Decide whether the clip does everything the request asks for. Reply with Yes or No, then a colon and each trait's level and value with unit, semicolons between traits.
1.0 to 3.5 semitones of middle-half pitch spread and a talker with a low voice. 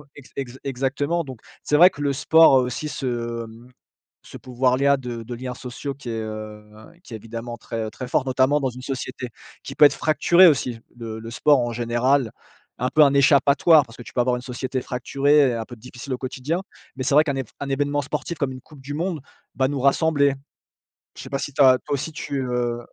Yes: average, 2.9 semitones; low, 130 Hz